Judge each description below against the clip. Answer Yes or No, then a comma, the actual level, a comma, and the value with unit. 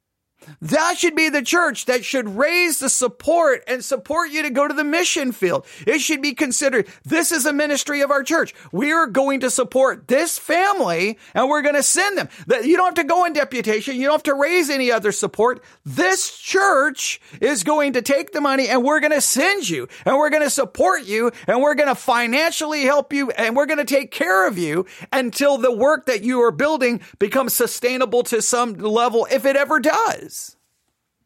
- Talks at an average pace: No, fast, 210 wpm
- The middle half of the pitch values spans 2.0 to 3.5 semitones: No, average, 3.9 semitones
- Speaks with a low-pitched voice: No, very high, 280 Hz